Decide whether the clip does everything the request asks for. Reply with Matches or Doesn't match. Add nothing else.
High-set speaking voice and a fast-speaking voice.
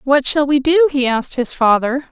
Matches